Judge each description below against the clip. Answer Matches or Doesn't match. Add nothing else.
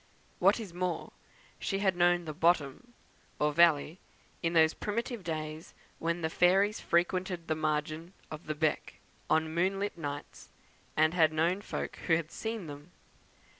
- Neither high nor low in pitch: Matches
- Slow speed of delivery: Doesn't match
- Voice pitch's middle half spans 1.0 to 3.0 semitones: Matches